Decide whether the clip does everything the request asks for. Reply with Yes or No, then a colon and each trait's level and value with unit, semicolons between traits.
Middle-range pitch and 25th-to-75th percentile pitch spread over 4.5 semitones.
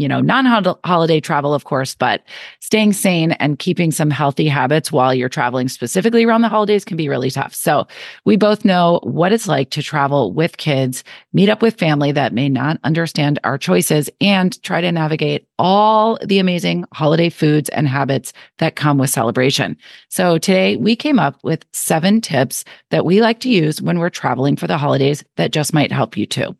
Yes: medium, 155 Hz; average, 5.2 semitones